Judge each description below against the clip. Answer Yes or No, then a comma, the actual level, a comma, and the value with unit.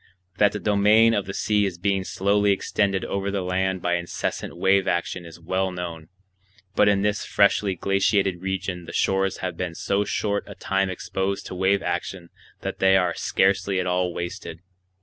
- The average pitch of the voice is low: Yes, very low, 95 Hz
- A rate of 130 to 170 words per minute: No, average, 180 wpm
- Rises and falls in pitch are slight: Yes, narrow, 1.8 semitones